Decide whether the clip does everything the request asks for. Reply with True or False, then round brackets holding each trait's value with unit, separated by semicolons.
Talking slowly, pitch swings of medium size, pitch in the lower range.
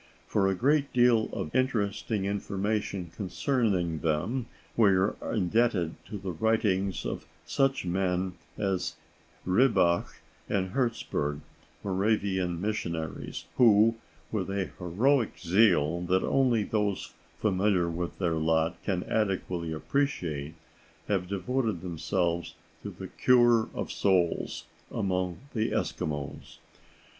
True (110 wpm; 4.1 semitones; 95 Hz)